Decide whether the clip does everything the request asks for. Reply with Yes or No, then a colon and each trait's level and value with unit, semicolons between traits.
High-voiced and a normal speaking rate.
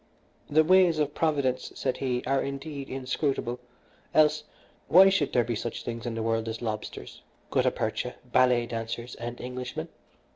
No: low, 130 Hz; average, 155 wpm